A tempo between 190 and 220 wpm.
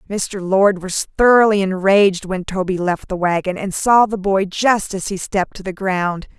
Yes: average, 195 wpm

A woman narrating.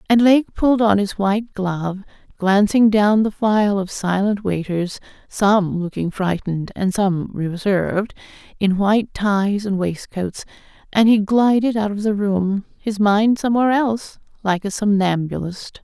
Yes: female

